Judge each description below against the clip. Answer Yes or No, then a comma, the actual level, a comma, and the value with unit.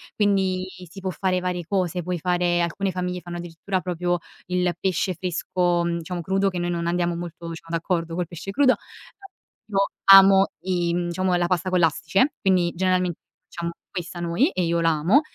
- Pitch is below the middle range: No, medium, 180 Hz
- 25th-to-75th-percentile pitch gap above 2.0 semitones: No, narrow, 1.6 semitones